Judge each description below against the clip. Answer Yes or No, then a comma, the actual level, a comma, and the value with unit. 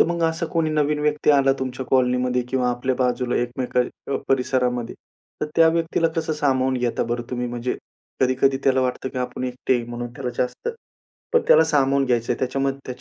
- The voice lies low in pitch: Yes, low, 130 Hz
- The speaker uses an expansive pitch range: No, average, 2.8 semitones